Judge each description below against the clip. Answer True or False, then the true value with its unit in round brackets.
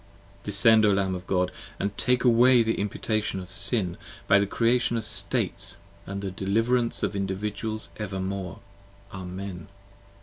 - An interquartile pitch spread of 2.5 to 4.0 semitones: True (2.9 semitones)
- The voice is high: False (100 Hz)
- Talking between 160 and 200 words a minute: False (140 wpm)